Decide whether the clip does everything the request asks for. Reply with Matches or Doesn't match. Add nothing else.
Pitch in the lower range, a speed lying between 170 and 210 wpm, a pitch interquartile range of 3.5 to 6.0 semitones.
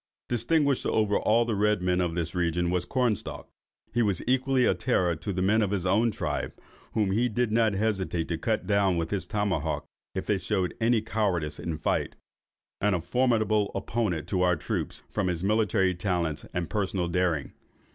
Matches